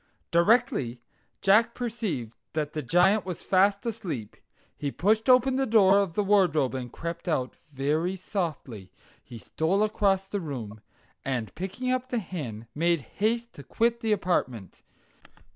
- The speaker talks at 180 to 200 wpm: No, average, 145 wpm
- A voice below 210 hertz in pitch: Yes, medium, 185 Hz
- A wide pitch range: Yes, wide, 7.2 semitones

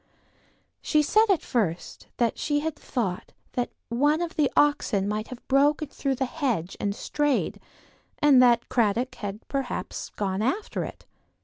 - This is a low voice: No, very high, 255 Hz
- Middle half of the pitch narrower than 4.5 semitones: No, wide, 5.4 semitones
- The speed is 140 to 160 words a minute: Yes, average, 150 wpm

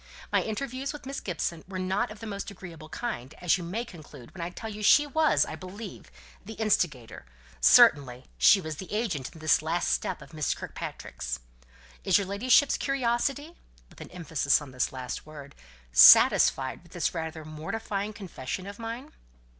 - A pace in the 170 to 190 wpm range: Yes, average, 175 wpm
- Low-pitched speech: No, medium, 185 Hz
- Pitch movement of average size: No, wide, 6.3 semitones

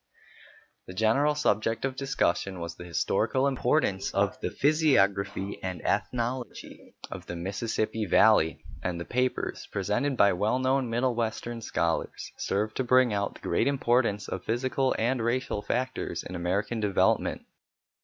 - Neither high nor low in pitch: No, low, 115 Hz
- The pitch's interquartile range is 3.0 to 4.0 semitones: No, average, 4.7 semitones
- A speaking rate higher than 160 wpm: No, average, 145 wpm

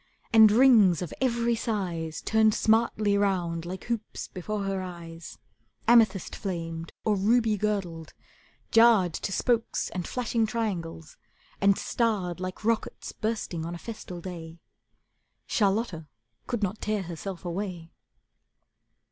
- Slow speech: Yes, slow, 120 wpm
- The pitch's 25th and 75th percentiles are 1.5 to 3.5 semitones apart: No, average, 4.3 semitones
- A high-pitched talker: Yes, high, 200 Hz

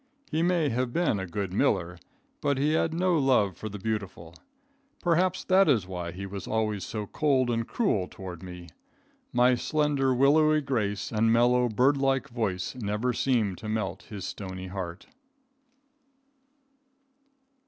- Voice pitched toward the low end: Yes, low, 115 Hz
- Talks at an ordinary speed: Yes, average, 150 wpm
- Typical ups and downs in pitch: No, wide, 6.0 semitones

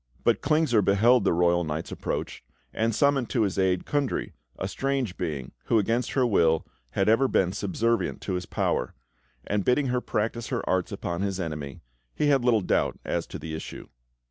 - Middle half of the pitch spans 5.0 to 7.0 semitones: Yes, wide, 5.6 semitones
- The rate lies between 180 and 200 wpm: Yes, average, 185 wpm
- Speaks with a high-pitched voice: No, low, 105 Hz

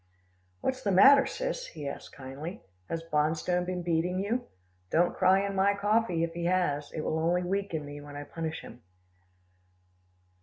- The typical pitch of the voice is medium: Yes, medium, 175 Hz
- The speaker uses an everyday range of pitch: Yes, average, 4.0 semitones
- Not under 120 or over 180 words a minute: Yes, average, 165 wpm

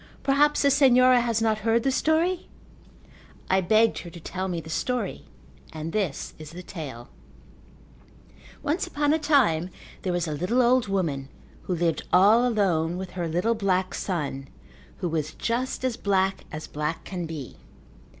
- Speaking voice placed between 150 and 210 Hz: Yes, high, 190 Hz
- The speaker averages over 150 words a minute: Yes, average, 160 wpm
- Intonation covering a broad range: Yes, wide, 6.8 semitones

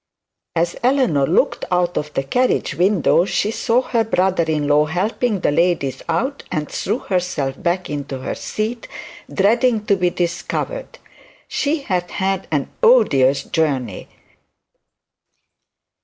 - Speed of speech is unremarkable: No, slow, 130 wpm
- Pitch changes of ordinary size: No, wide, 6.6 semitones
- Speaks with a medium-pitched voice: Yes, medium, 180 Hz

